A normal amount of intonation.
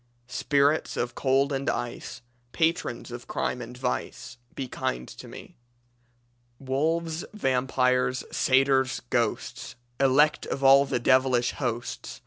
No: narrow, 1.9 semitones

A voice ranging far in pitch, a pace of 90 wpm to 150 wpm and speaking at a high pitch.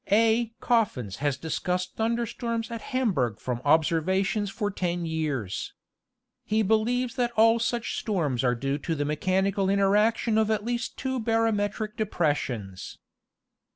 Yes: wide, 6.7 semitones; slow, 135 wpm; high, 205 Hz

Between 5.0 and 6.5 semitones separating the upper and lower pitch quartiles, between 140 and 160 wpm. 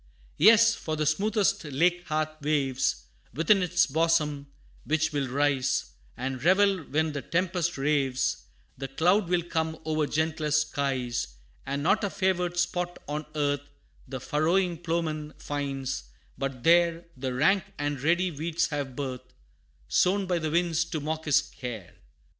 No: average, 3.6 semitones; average, 145 wpm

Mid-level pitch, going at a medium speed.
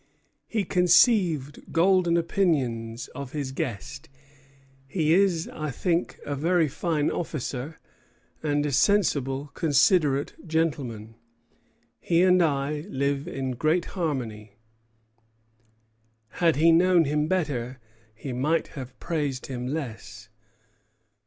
No: medium, 150 Hz; slow, 105 wpm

